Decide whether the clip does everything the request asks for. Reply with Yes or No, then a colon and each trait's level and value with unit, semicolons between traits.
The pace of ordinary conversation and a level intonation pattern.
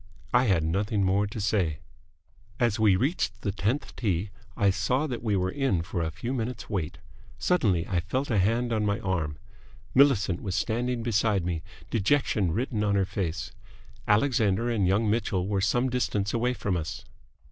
No: average, 175 wpm; average, 4.1 semitones